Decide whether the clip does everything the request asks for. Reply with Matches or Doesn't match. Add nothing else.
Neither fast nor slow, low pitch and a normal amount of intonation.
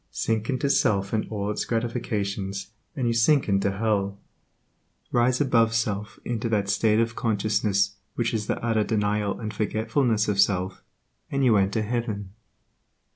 Doesn't match